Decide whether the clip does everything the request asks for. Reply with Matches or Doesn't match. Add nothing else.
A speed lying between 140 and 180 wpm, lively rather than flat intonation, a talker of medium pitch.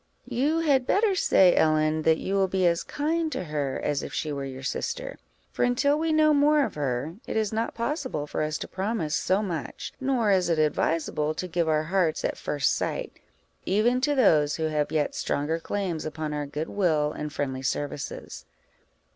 Doesn't match